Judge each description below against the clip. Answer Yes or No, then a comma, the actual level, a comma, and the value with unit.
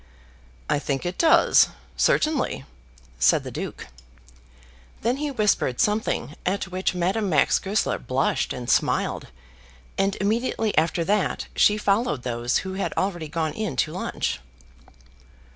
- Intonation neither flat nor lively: No, wide, 5.9 semitones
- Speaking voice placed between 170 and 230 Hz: Yes, high, 190 Hz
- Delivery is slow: Yes, slow, 130 wpm